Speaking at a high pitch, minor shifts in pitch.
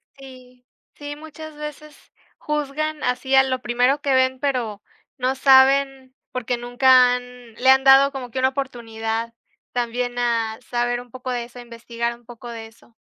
Yes: very high, 250 Hz; narrow, 2.0 semitones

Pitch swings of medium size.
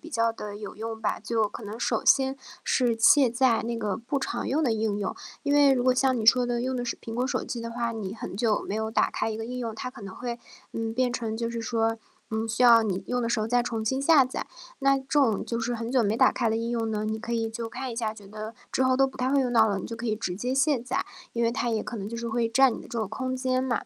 No: narrow, 2.3 semitones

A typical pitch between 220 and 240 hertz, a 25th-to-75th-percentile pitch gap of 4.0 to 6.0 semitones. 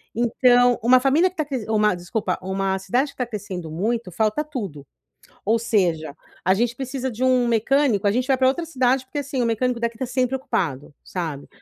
Yes: high, 235 Hz; average, 5.0 semitones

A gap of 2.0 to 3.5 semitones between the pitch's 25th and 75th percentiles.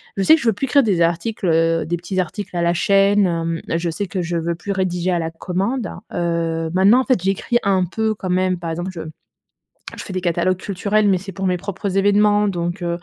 Yes: average, 2.8 semitones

